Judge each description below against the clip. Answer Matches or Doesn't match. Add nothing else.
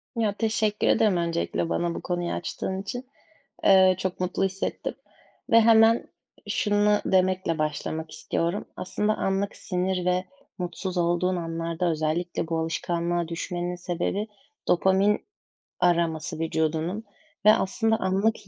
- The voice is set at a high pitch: Doesn't match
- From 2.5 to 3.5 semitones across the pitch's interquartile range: Matches